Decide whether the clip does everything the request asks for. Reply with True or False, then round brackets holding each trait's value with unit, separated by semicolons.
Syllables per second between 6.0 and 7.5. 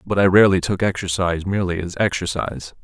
True (6.8 syllables/s)